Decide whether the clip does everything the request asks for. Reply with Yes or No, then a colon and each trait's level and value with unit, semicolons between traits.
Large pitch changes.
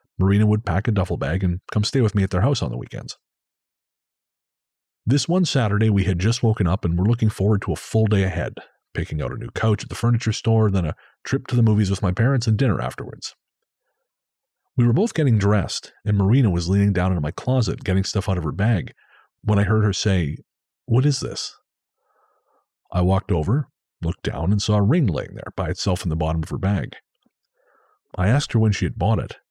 No: average, 3.6 semitones